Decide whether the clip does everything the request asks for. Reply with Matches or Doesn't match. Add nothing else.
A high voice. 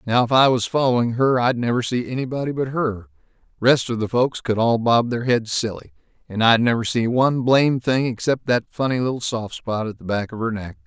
Doesn't match